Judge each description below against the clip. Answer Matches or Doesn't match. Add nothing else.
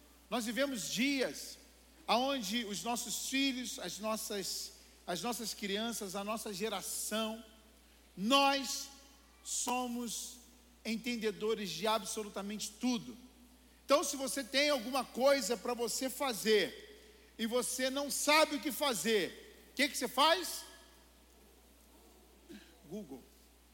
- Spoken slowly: Matches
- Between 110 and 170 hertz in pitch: Doesn't match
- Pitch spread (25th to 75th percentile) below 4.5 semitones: Matches